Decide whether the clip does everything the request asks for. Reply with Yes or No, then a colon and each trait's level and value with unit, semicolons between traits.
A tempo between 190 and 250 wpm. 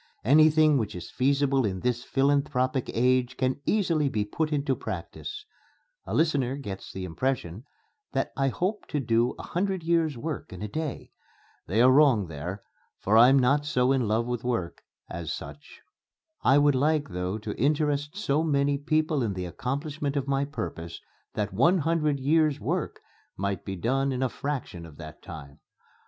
No: average, 170 wpm